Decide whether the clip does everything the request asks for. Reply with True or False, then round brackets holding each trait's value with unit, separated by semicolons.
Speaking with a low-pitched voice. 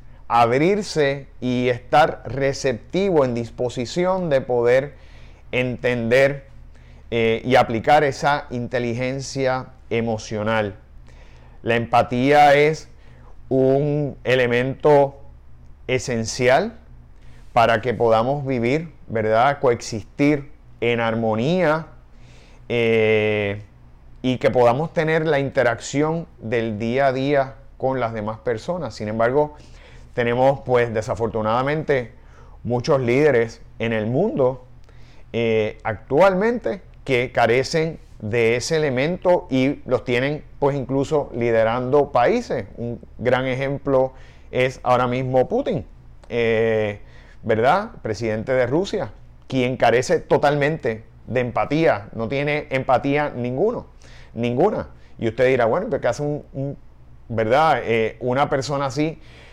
True (120 Hz)